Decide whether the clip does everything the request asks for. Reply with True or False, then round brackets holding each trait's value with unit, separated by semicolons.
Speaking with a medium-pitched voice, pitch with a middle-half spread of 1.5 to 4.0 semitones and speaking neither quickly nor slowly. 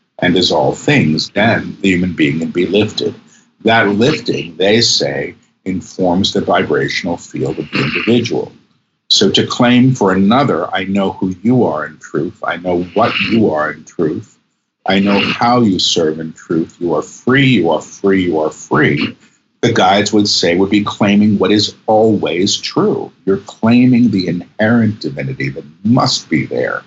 False (100 Hz; 3.3 semitones; 170 wpm)